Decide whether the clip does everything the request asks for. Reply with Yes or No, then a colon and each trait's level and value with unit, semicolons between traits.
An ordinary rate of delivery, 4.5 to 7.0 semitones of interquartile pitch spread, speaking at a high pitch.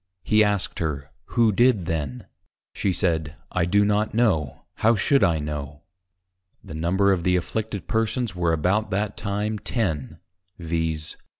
No: average, 145 wpm; average, 5.0 semitones; very low, 95 Hz